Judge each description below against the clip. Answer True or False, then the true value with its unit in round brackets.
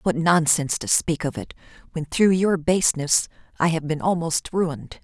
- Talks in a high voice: False (165 Hz)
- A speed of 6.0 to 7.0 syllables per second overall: False (5.0 syllables/s)